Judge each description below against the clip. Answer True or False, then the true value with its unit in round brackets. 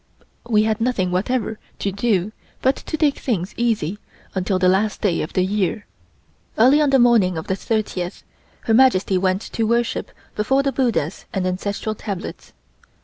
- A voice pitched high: True (210 Hz)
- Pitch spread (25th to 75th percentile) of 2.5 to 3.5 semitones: False (4.3 semitones)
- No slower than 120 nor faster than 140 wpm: False (165 wpm)